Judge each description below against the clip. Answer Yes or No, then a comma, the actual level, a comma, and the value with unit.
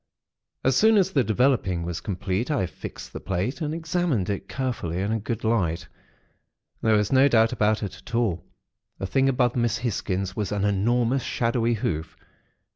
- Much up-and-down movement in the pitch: No, average, 4.8 semitones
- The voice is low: Yes, low, 115 Hz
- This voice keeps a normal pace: Yes, average, 175 wpm